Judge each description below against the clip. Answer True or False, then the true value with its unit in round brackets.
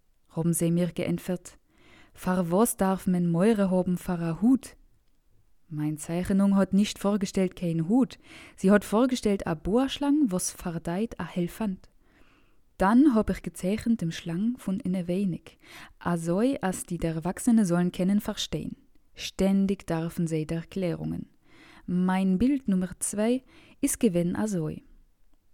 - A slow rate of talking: False (135 wpm)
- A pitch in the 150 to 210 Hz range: True (185 Hz)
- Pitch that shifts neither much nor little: True (3.6 semitones)